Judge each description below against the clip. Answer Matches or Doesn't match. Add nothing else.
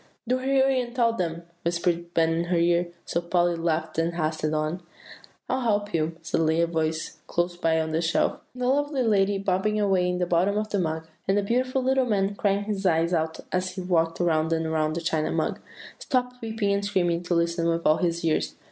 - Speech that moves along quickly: Matches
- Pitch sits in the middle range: Matches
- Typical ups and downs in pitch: Matches